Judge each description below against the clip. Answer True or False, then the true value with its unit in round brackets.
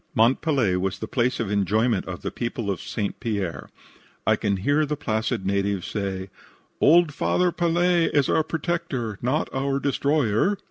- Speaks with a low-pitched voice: True (120 Hz)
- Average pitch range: False (6.9 semitones)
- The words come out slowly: False (165 wpm)